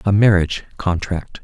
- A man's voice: Yes, male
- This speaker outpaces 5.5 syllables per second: No, 5.1 syllables/s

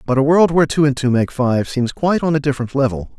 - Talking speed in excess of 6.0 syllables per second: Yes, 6.6 syllables/s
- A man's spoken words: Yes, male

